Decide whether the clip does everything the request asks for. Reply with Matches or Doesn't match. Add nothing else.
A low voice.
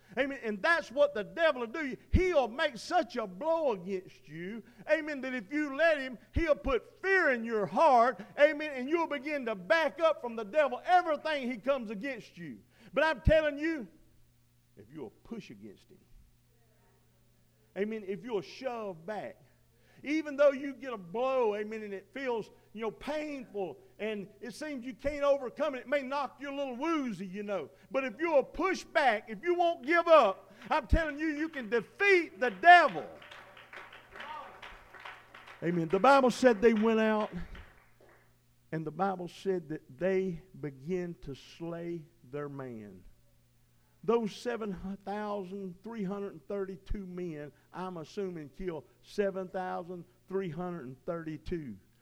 Doesn't match